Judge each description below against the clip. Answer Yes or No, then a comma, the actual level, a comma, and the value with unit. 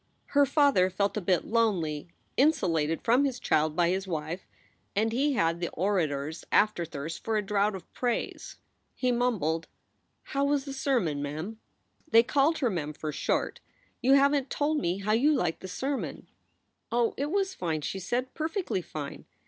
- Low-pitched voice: No, high, 210 Hz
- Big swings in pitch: Yes, wide, 8.4 semitones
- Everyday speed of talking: Yes, average, 175 wpm